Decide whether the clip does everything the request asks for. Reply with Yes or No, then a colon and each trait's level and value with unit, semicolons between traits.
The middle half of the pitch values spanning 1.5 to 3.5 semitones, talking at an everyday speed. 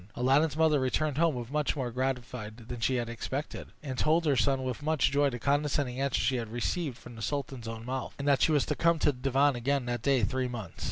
No: average, 2.9 semitones; fast, 235 wpm